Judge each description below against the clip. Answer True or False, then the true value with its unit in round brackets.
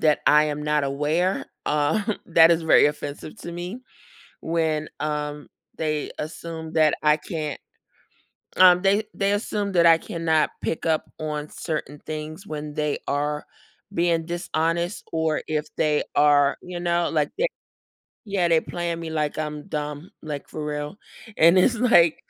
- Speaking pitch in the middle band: True (160 Hz)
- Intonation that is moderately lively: False (2.3 semitones)